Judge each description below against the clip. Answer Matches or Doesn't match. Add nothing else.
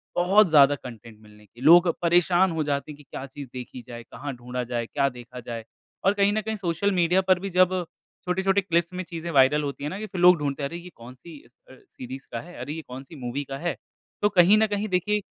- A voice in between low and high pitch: Matches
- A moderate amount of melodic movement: Doesn't match